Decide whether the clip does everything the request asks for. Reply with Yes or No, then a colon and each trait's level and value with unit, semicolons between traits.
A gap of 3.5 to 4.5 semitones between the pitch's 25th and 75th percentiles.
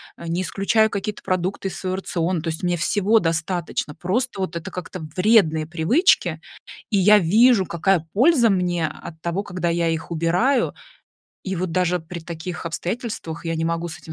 No: average, 3.1 semitones